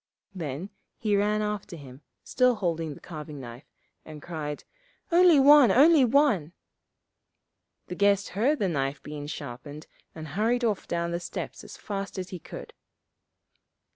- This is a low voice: No, medium, 180 Hz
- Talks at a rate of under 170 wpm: Yes, average, 150 wpm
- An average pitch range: No, wide, 6.3 semitones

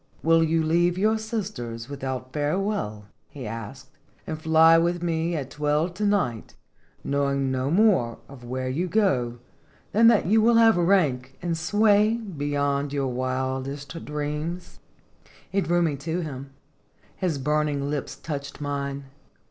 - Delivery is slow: No, average, 150 wpm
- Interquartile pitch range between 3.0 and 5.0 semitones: Yes, average, 4.4 semitones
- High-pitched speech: No, medium, 150 Hz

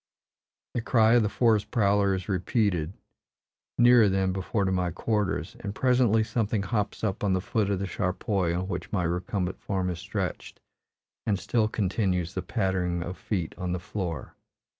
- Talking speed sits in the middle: Yes, average, 170 wpm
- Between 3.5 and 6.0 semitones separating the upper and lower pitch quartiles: No, average, 3.1 semitones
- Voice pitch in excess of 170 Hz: No, low, 100 Hz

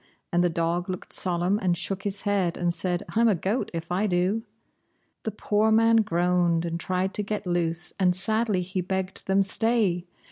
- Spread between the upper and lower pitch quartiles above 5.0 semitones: No, average, 2.9 semitones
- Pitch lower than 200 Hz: Yes, medium, 185 Hz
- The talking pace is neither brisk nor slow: Yes, average, 185 wpm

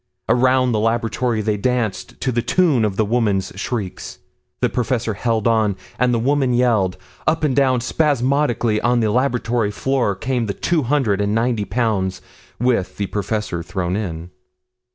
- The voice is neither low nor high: No, low, 115 Hz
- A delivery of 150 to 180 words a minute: Yes, average, 160 wpm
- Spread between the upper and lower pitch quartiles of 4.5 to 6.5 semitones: No, average, 3.5 semitones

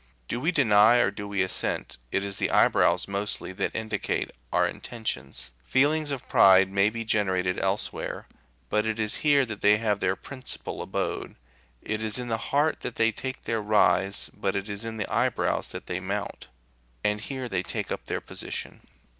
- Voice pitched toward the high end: No, low, 105 Hz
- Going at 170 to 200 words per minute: Yes, average, 185 wpm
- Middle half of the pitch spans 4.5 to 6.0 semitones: No, average, 3.2 semitones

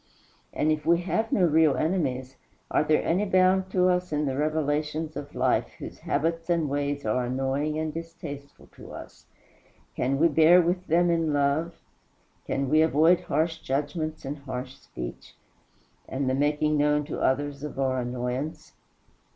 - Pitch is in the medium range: Yes, medium, 150 Hz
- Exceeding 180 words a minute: No, average, 160 wpm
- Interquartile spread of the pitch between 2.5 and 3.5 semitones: Yes, average, 2.9 semitones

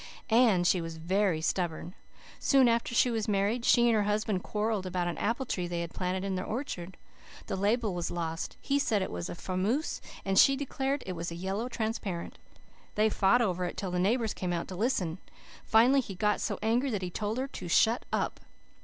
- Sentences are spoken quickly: Yes, fast, 215 wpm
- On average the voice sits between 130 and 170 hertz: No, high, 200 Hz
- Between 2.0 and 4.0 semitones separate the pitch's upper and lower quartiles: No, average, 4.4 semitones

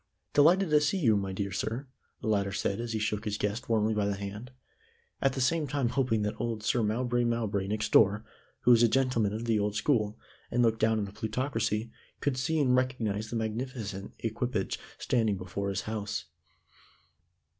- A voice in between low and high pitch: No, low, 110 Hz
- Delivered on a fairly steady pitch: No, average, 3.3 semitones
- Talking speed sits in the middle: Yes, average, 190 wpm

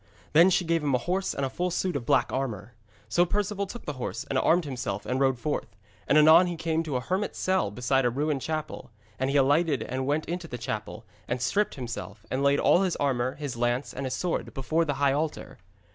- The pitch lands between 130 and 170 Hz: Yes, medium, 140 Hz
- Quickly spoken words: Yes, fast, 230 wpm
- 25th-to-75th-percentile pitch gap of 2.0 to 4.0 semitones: No, average, 4.7 semitones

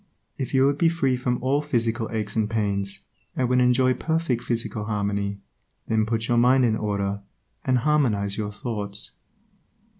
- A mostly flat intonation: No, average, 3.7 semitones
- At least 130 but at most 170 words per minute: Yes, average, 160 wpm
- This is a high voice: No, low, 115 Hz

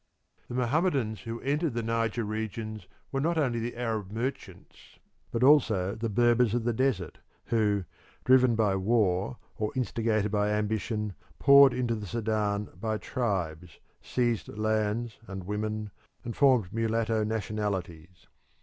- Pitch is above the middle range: No, low, 110 Hz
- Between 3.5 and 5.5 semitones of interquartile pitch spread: No, narrow, 2.5 semitones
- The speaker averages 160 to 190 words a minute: No, slow, 135 wpm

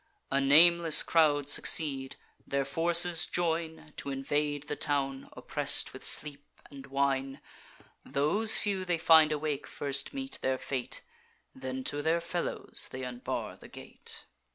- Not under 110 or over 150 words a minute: Yes, slow, 135 wpm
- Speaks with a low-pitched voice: No, medium, 145 Hz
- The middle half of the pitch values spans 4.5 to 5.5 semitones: No, average, 3.3 semitones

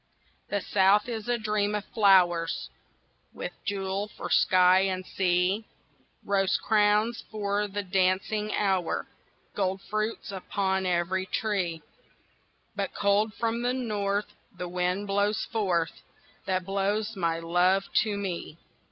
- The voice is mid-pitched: No, high, 200 Hz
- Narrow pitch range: Yes, narrow, 2.2 semitones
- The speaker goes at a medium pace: No, slow, 125 wpm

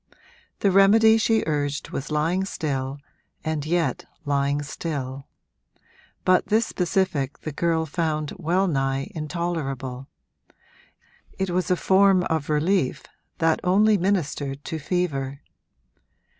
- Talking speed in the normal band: No, slow, 115 wpm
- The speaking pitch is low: No, medium, 160 Hz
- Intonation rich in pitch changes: No, average, 4.5 semitones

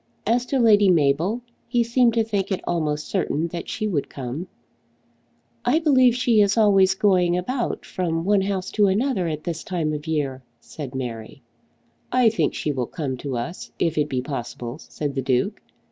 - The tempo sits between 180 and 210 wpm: Yes, average, 185 wpm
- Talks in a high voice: No, medium, 180 Hz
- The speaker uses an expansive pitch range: Yes, wide, 6.4 semitones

